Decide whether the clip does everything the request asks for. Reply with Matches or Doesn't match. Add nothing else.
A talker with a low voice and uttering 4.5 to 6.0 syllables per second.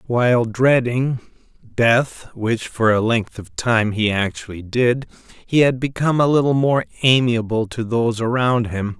Doesn't match